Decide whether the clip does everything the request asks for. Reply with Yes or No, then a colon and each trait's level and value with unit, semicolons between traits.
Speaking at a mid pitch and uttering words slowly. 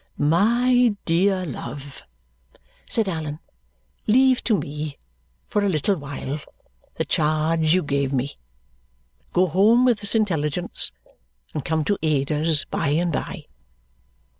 Yes: medium, 165 Hz; slow, 120 wpm